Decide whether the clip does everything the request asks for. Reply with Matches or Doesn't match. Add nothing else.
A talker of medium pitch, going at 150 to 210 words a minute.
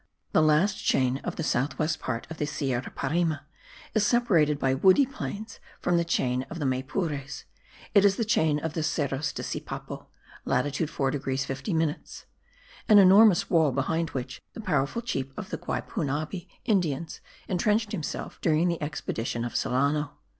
Matches